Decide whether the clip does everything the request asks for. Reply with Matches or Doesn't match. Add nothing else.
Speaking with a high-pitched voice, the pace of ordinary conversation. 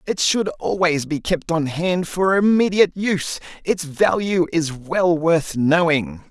Doesn't match